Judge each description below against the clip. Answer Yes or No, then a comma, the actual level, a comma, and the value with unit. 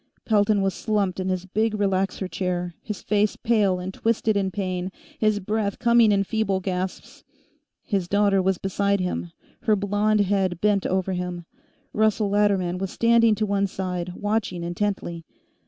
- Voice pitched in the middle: No, high, 195 Hz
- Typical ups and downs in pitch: No, narrow, 2.3 semitones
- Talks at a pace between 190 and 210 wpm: No, average, 155 wpm